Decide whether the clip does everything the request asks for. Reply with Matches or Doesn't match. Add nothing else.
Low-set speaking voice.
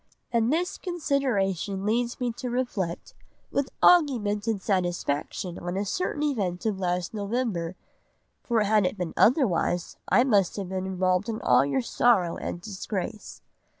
Doesn't match